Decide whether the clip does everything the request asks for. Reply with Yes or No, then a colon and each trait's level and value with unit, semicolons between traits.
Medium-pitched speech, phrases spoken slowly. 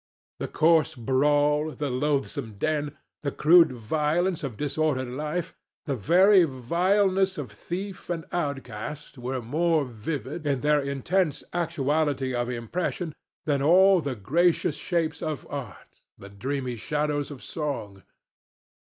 Yes: medium, 150 Hz; slow, 125 wpm